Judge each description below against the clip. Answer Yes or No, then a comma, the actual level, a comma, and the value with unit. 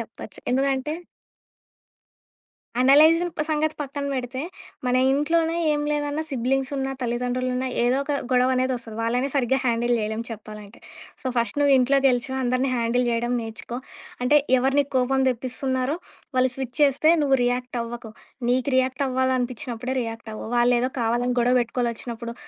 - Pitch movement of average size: No, narrow, 2.2 semitones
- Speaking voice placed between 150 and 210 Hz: No, very high, 255 Hz